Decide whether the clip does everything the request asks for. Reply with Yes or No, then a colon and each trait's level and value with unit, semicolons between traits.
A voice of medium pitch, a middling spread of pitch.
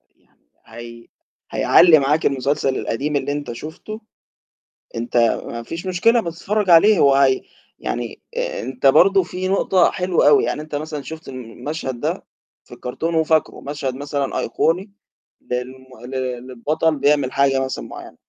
Yes: medium, 145 Hz; average, 4.3 semitones